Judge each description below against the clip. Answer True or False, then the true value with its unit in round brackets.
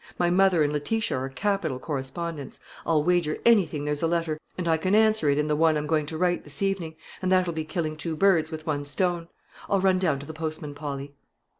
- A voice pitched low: False (160 Hz)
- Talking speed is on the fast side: True (225 wpm)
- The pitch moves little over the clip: False (3.3 semitones)